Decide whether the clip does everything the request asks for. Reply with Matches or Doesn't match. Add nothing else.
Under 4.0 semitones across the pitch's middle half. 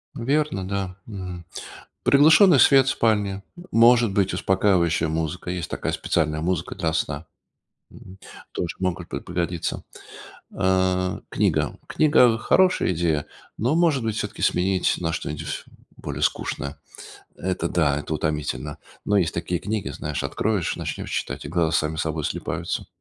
Doesn't match